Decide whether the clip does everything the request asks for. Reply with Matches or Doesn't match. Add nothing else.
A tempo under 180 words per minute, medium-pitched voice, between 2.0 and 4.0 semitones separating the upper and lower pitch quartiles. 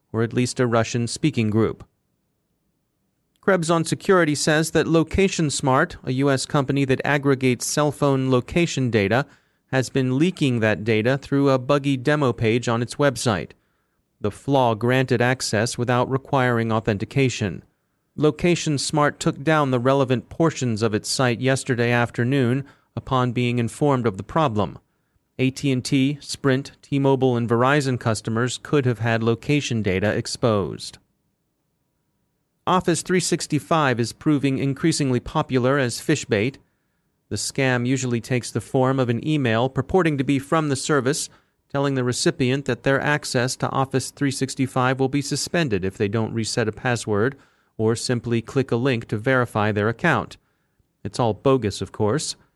Doesn't match